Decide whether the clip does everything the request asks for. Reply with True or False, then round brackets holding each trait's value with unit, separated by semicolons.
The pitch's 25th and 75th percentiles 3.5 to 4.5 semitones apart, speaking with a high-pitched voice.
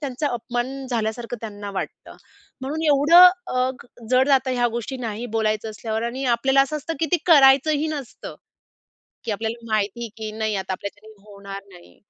True (4.0 semitones; 240 Hz)